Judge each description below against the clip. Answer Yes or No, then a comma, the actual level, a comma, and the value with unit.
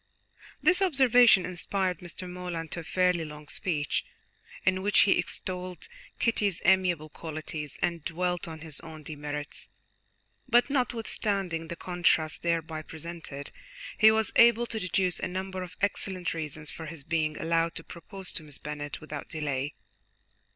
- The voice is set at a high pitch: No, medium, 170 Hz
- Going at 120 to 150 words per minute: Yes, average, 145 wpm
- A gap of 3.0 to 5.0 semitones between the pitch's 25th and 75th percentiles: Yes, average, 3.3 semitones